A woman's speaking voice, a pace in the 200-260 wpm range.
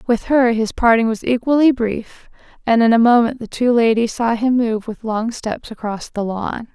Yes: female; fast, 205 wpm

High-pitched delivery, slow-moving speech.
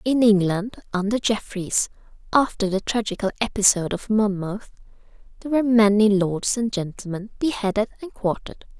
Yes: high, 210 Hz; slow, 130 wpm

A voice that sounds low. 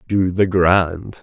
Yes: very low, 90 Hz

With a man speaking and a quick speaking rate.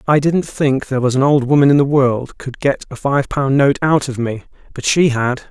Yes: male; fast, 250 wpm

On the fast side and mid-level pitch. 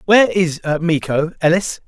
No: slow, 130 wpm; medium, 170 Hz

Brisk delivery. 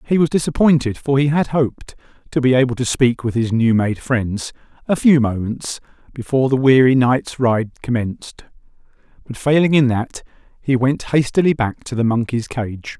No: average, 175 wpm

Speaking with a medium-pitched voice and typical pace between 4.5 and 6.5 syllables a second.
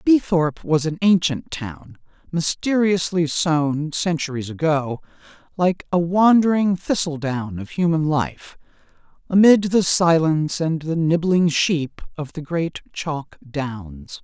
No: medium, 165 Hz; 3.8 syllables/s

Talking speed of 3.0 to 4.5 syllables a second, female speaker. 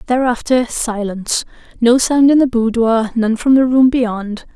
Yes: 4.4 syllables/s; female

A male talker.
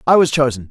Yes: male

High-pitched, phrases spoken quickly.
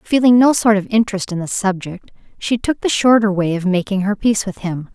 Yes: high, 205 Hz; fast, 230 wpm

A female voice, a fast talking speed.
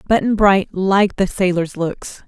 No: female; average, 160 wpm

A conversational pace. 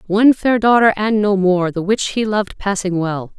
No: fast, 215 wpm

